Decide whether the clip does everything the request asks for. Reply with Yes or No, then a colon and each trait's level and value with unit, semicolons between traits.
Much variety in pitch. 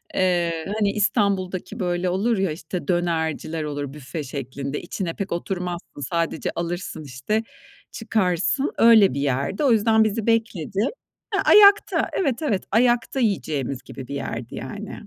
Yes: wide, 5.9 semitones